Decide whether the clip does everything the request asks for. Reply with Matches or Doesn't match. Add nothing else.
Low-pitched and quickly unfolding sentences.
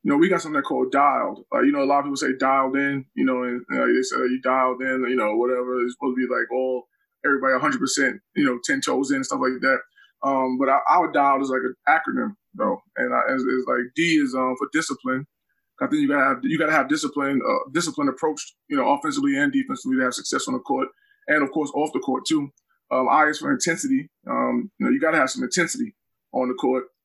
Doesn't match